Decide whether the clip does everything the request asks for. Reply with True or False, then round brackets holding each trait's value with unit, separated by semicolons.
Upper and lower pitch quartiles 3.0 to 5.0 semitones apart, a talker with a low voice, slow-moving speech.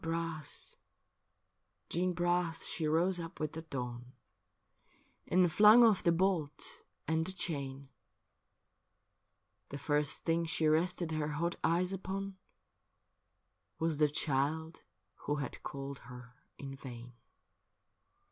False (3.5 semitones; 160 Hz; 120 wpm)